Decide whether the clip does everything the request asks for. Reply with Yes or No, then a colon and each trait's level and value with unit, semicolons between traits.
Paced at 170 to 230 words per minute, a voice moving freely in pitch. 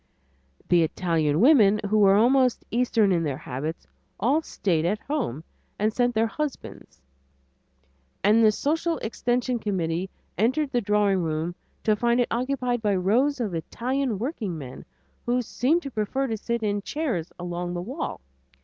No: average, 150 wpm; wide, 5.9 semitones